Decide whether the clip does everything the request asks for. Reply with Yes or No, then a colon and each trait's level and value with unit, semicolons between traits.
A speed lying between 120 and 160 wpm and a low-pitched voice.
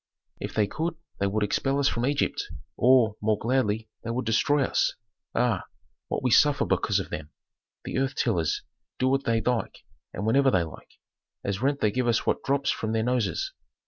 No: average, 190 wpm; low, 120 Hz